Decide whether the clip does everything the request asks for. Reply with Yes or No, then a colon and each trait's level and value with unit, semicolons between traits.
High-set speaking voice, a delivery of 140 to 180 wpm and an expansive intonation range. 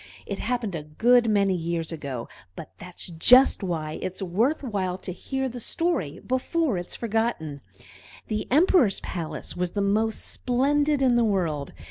Yes: high, 200 Hz; average, 160 wpm; wide, 6.4 semitones